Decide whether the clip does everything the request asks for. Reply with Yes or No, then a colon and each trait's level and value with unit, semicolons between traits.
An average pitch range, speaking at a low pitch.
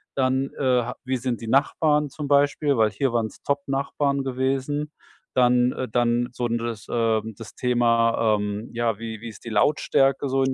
Yes: average, 3.0 semitones; low, 125 Hz